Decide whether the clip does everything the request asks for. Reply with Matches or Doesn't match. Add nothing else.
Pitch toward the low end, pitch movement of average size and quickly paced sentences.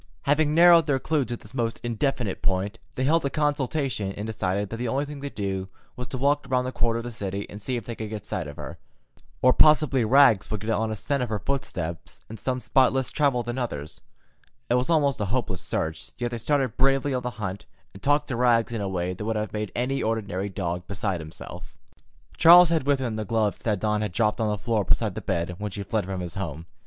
Matches